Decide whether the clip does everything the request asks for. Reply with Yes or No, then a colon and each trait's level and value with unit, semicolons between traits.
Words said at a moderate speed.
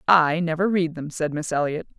No: fast, 210 wpm